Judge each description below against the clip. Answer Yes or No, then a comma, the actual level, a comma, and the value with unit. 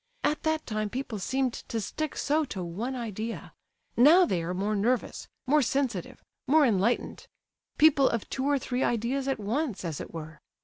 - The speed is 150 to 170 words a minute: Yes, average, 165 wpm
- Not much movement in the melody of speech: No, average, 5.2 semitones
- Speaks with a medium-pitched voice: No, high, 240 Hz